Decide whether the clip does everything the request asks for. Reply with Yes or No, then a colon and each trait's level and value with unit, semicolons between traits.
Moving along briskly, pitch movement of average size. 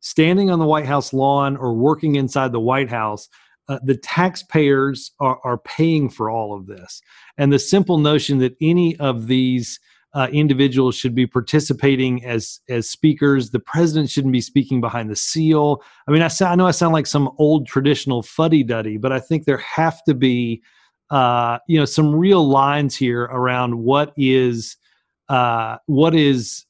No: average, 180 wpm; average, 3.5 semitones